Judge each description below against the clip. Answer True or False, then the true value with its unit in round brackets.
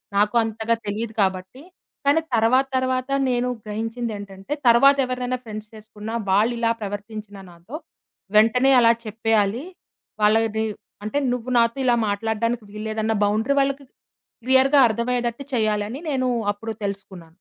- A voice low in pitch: False (225 Hz)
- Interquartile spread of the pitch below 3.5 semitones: True (3.1 semitones)